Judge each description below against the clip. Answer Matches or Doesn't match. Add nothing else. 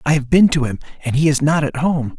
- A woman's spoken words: Doesn't match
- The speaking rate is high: Matches